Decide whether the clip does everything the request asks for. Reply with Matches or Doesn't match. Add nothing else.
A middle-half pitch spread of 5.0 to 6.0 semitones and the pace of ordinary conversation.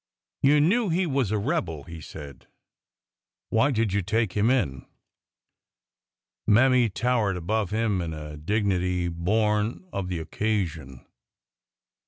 Doesn't match